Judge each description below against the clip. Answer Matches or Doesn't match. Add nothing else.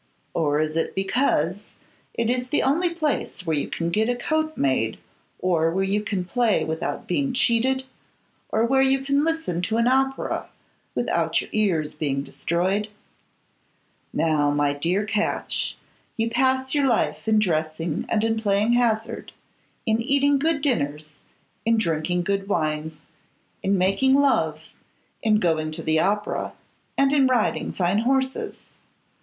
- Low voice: Doesn't match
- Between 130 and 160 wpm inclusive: Matches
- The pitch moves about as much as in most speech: Doesn't match